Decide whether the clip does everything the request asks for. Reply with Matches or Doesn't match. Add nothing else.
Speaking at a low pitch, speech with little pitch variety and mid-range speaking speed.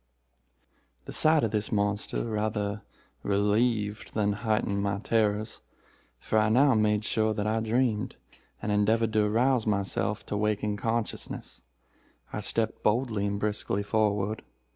Doesn't match